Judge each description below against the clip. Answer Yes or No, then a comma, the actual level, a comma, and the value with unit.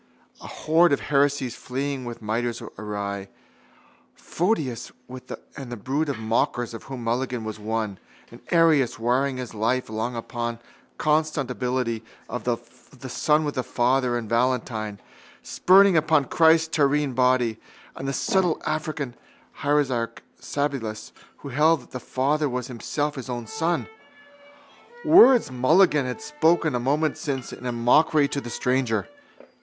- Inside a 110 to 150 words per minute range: Yes, average, 140 wpm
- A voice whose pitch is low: Yes, low, 130 Hz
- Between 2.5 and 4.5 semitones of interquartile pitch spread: Yes, average, 3.8 semitones